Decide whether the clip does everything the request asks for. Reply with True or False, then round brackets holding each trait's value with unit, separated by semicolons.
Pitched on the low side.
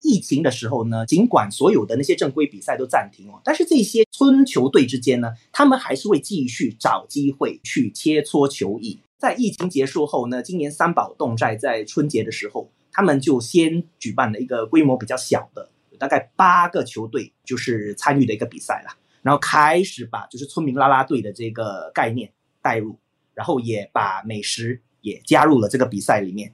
True (130 Hz)